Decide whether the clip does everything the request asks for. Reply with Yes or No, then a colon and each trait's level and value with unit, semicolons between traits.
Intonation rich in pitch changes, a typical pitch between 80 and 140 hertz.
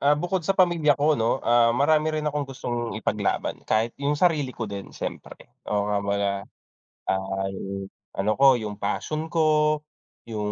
Yes: wide, 6.7 semitones; low, 135 Hz